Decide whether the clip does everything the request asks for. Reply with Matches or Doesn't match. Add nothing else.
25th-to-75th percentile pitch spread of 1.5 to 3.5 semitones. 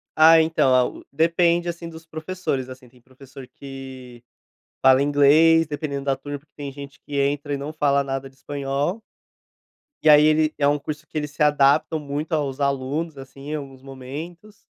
Matches